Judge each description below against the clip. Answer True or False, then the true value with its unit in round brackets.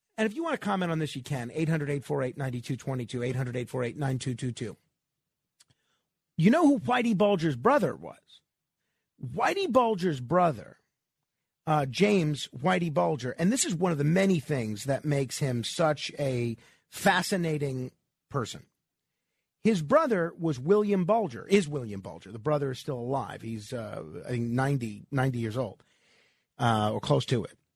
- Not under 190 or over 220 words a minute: False (155 wpm)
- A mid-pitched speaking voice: True (145 Hz)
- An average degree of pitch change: False (6.1 semitones)